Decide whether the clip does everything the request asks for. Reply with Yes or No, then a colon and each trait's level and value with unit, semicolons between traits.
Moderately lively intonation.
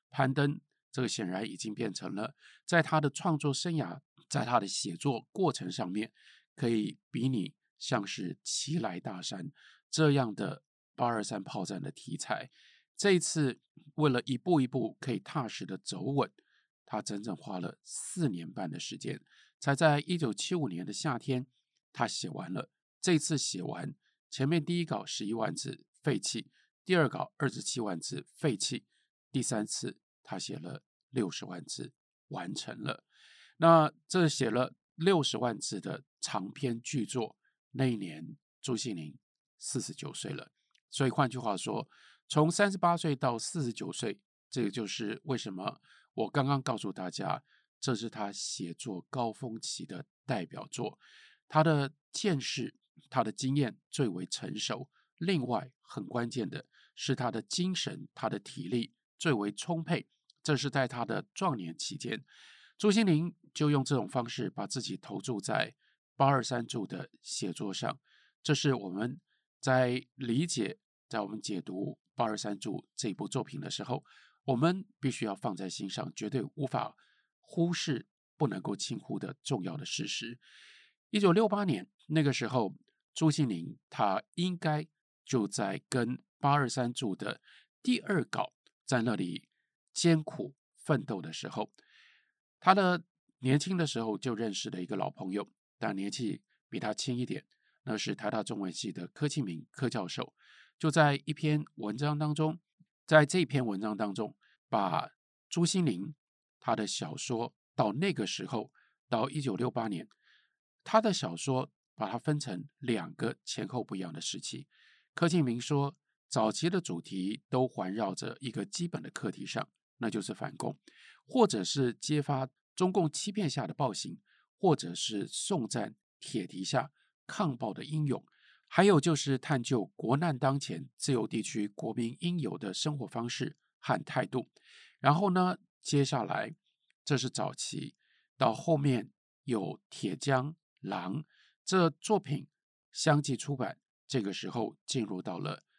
Yes: average, 5.0 semitones